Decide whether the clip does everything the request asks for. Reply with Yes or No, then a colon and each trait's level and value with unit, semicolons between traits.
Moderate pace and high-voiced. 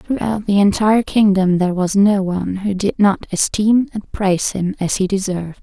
Yes: average, 190 wpm; high, 195 Hz